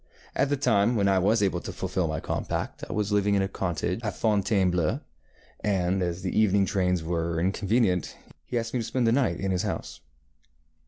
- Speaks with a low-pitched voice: Yes, low, 100 Hz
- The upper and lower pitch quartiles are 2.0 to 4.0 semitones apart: Yes, average, 3.2 semitones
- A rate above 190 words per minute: Yes, average, 200 wpm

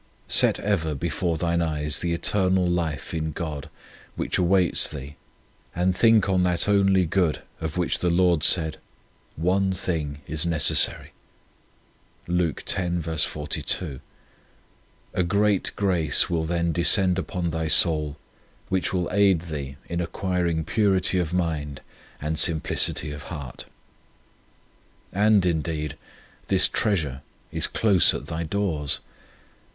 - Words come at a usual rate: No, slow, 125 wpm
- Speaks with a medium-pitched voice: No, very low, 85 Hz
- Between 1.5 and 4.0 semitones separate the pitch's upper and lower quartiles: Yes, average, 2.9 semitones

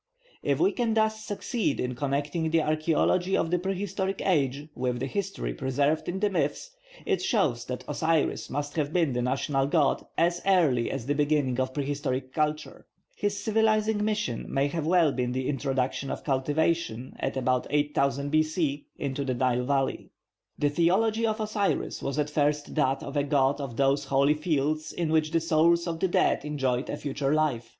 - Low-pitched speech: No, medium, 150 Hz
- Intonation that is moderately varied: Yes, average, 4.2 semitones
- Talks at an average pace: Yes, average, 180 wpm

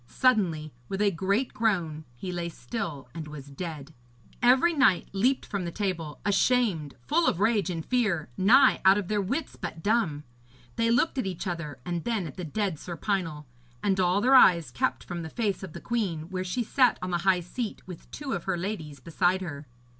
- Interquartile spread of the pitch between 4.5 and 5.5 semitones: Yes, average, 5.0 semitones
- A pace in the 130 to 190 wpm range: No, average, 200 wpm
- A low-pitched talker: No, medium, 185 Hz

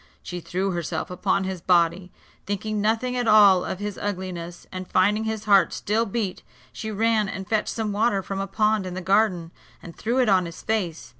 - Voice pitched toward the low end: No, high, 195 Hz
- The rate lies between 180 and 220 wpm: Yes, average, 200 wpm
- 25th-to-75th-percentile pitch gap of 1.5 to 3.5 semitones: Yes, average, 2.9 semitones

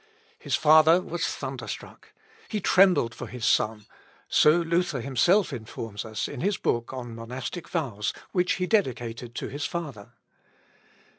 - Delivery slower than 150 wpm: Yes, average, 140 wpm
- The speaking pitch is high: No, medium, 140 Hz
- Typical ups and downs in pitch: No, wide, 7.0 semitones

